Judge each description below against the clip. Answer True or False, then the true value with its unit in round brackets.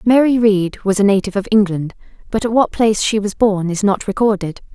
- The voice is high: True (205 Hz)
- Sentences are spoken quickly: True (215 wpm)